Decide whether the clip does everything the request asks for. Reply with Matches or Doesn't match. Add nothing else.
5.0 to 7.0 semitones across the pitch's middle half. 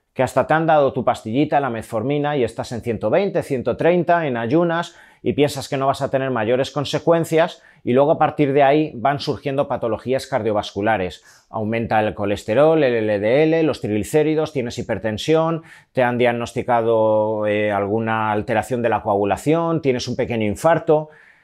Matches